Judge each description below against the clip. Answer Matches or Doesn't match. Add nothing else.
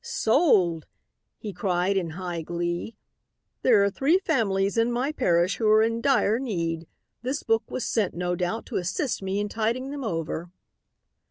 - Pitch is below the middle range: Doesn't match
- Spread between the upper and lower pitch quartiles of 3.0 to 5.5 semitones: Matches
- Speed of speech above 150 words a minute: Matches